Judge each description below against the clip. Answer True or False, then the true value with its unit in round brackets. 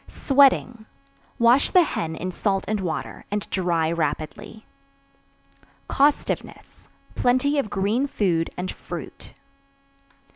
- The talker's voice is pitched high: True (210 Hz)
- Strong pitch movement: True (6.6 semitones)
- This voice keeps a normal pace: False (105 wpm)